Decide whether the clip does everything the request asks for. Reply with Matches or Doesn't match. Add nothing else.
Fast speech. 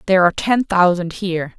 Doesn't match